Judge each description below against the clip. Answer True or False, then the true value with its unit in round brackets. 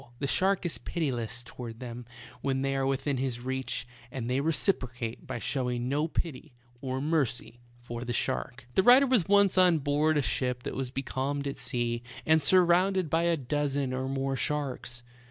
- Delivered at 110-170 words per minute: False (180 wpm)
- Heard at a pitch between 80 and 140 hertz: True (135 Hz)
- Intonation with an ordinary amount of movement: True (4.0 semitones)